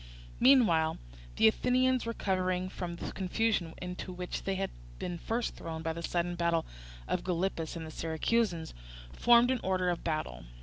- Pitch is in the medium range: Yes, medium, 180 Hz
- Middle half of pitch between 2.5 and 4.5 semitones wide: No, average, 4.9 semitones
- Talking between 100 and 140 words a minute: No, average, 160 wpm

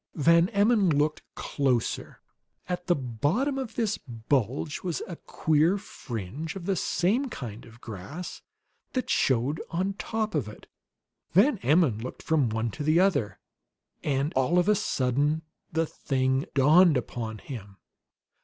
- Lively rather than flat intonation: Yes, wide, 6.4 semitones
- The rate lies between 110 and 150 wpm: Yes, average, 145 wpm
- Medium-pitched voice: Yes, medium, 150 Hz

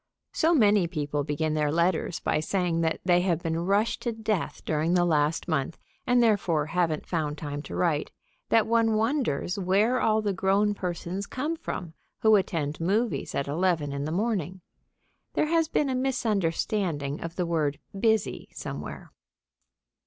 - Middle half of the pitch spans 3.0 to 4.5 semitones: No, wide, 5.5 semitones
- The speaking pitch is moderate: Yes, medium, 180 Hz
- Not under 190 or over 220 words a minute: No, average, 160 wpm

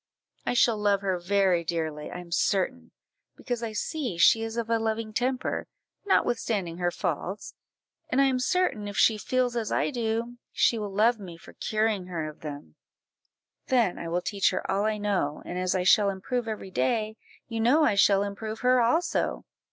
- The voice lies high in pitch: Yes, high, 215 Hz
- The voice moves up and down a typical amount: Yes, average, 4.2 semitones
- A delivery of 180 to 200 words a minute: Yes, average, 190 wpm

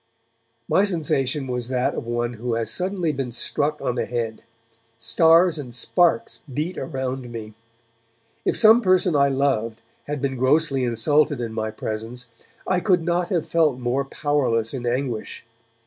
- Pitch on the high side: No, low, 135 Hz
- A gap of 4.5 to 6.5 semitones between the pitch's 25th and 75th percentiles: Yes, average, 5.3 semitones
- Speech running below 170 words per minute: Yes, average, 155 wpm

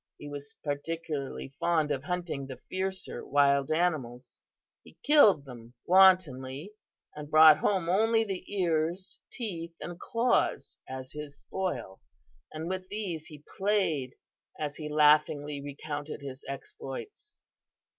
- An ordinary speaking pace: No, slow, 125 wpm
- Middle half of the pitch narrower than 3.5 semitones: No, average, 4.7 semitones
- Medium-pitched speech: Yes, medium, 155 Hz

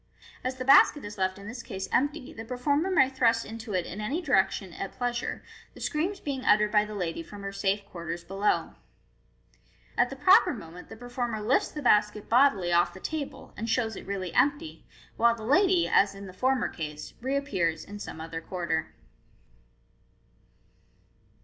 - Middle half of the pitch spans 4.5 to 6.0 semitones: Yes, wide, 5.6 semitones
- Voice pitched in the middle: No, high, 215 Hz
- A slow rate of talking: No, average, 175 wpm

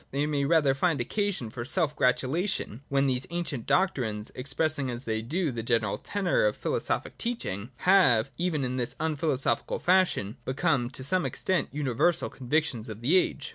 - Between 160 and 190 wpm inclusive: Yes, average, 170 wpm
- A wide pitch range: Yes, wide, 6.0 semitones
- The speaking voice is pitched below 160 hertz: Yes, medium, 140 Hz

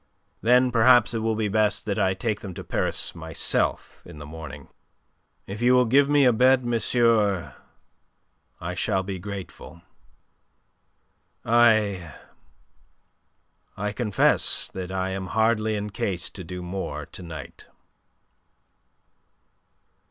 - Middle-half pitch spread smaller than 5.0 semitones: Yes, average, 3.9 semitones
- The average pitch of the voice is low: Yes, low, 105 Hz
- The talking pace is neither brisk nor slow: No, slow, 125 wpm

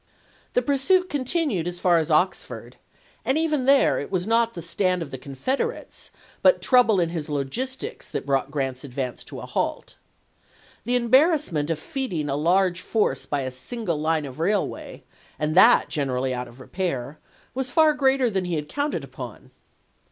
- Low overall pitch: No, medium, 180 Hz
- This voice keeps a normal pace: Yes, average, 175 wpm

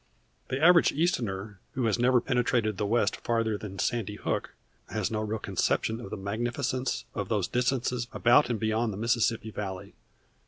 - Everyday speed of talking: Yes, average, 165 wpm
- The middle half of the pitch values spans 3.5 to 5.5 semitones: No, average, 2.7 semitones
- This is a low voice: Yes, low, 115 Hz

